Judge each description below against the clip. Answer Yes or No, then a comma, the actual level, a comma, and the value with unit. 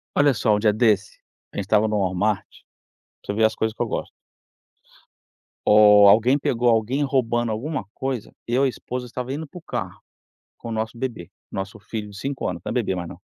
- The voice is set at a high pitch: No, low, 110 Hz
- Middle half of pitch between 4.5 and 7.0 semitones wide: No, average, 3.3 semitones